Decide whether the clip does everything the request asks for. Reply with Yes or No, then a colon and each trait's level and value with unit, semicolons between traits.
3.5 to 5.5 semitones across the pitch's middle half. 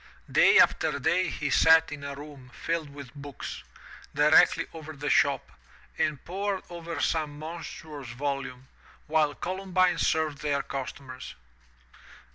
No: average, 2.7 semitones